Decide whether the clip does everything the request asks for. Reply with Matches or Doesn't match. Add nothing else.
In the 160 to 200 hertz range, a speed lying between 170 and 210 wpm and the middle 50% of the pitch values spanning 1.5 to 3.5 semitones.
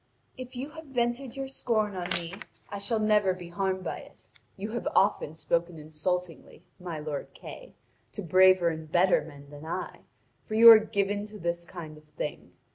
Doesn't match